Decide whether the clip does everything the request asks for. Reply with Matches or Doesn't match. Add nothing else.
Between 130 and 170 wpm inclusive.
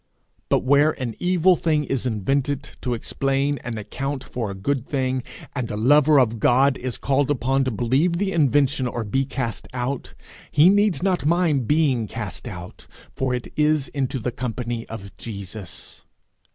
Matches